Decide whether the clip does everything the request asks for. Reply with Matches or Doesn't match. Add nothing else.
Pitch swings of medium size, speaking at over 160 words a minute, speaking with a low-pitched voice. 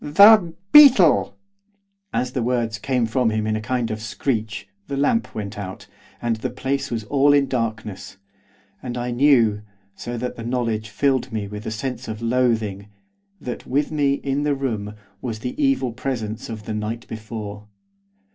Matches